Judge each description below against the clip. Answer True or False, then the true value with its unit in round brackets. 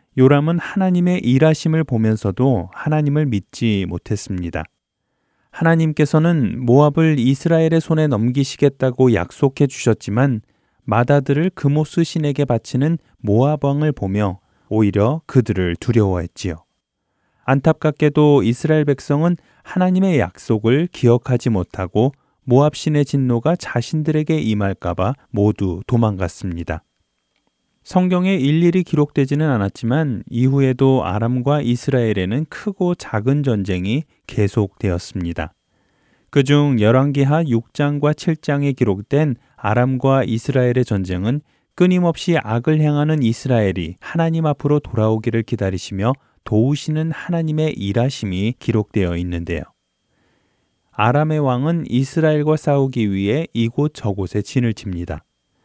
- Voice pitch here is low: True (130 Hz)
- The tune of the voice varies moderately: False (5.9 semitones)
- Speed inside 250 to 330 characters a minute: True (300 characters per minute)